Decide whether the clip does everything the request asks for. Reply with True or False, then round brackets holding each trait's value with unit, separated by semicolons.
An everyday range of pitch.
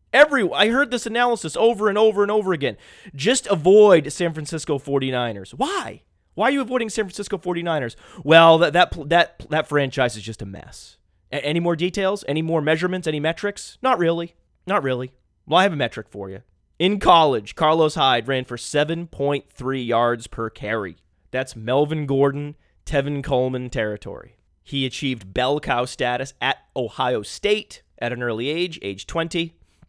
False (6.3 semitones)